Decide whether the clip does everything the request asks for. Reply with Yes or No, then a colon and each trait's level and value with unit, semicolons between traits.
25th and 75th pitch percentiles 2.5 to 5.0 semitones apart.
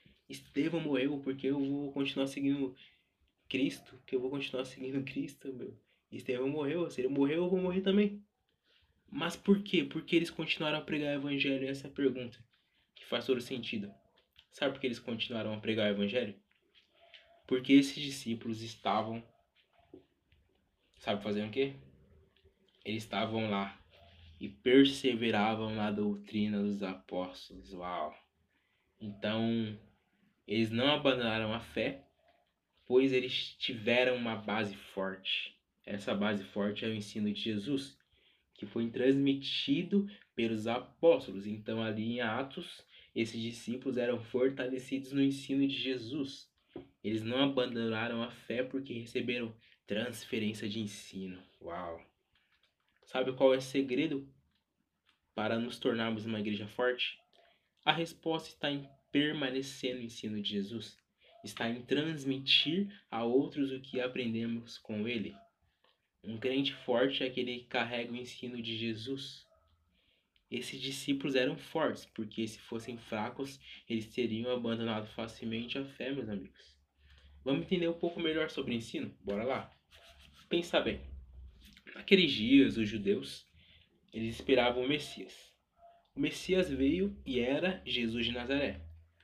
Yes: average, 4.1 semitones